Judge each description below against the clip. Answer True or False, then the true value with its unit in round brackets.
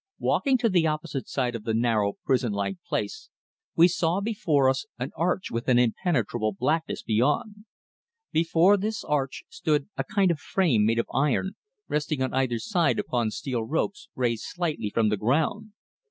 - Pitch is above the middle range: False (145 Hz)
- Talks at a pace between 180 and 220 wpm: False (170 wpm)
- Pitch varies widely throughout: True (6.9 semitones)